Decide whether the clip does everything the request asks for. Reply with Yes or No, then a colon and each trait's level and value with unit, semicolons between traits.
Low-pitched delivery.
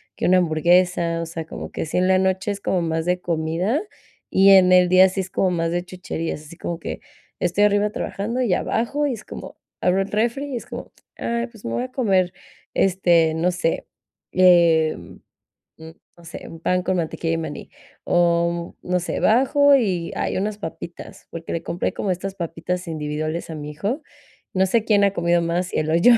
No: medium, 180 Hz